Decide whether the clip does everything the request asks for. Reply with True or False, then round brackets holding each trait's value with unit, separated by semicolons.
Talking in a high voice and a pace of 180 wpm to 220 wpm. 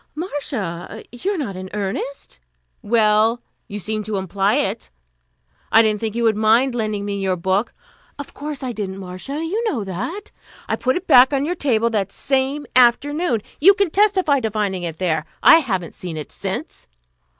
True (225 Hz; 185 wpm)